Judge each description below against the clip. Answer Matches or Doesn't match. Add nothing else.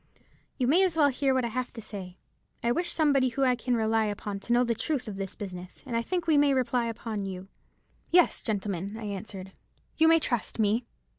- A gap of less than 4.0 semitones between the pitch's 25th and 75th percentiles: Doesn't match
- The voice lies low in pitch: Doesn't match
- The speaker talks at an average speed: Doesn't match